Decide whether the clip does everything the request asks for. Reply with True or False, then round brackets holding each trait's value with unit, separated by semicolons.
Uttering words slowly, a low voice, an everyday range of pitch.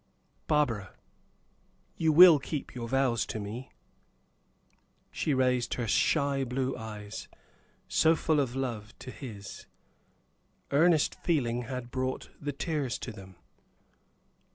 True (115 wpm; 130 Hz; 3.7 semitones)